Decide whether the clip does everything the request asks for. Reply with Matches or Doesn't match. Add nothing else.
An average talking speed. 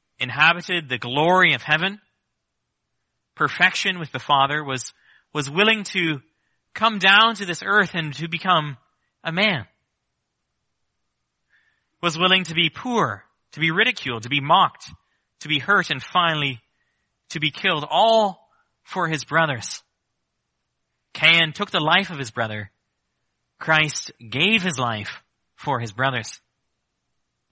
Doesn't match